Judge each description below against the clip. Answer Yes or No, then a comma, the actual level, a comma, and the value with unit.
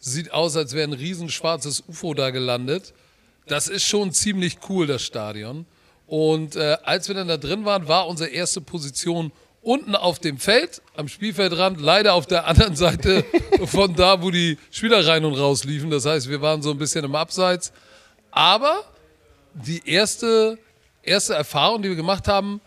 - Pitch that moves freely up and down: No, average, 4.1 semitones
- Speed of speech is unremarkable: Yes, average, 175 wpm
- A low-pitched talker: No, medium, 170 Hz